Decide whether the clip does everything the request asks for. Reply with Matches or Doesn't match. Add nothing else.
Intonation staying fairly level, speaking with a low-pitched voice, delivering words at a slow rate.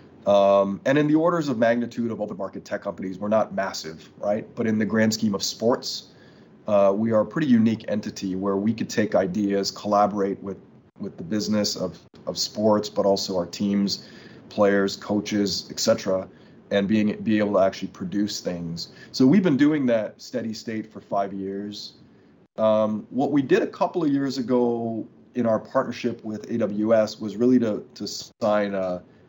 Doesn't match